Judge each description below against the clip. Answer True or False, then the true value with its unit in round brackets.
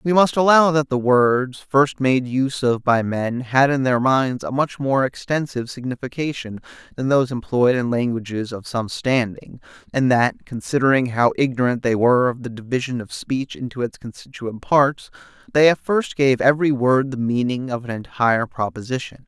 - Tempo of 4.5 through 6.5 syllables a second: True (5.0 syllables/s)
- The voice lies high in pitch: False (130 Hz)